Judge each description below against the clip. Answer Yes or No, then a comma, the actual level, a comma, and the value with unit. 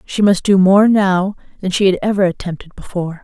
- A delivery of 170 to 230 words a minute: Yes, fast, 205 wpm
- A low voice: No, high, 190 Hz